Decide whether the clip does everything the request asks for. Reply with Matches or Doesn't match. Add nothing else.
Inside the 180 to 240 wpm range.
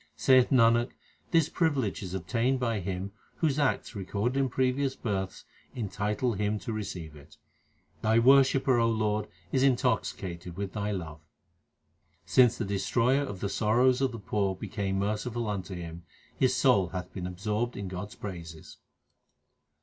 Doesn't match